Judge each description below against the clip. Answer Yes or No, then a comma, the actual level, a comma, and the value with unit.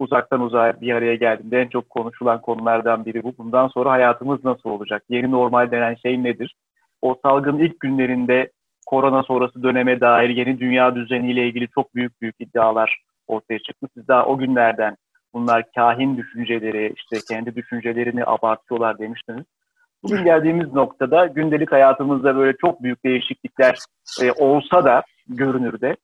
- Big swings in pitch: No, narrow, 2.4 semitones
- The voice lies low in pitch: Yes, low, 125 Hz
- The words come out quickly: Yes, fast, 150 wpm